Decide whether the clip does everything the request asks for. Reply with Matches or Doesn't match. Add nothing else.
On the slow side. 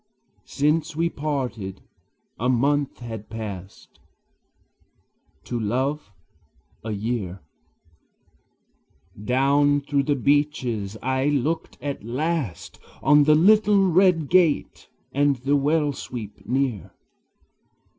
Matches